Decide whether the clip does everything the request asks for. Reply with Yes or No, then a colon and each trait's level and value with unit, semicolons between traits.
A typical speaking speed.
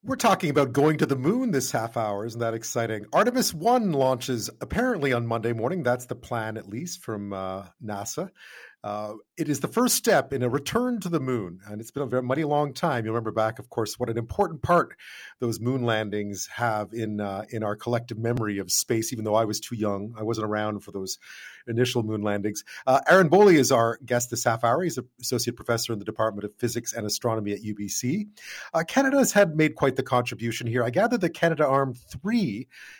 No: fast, 220 wpm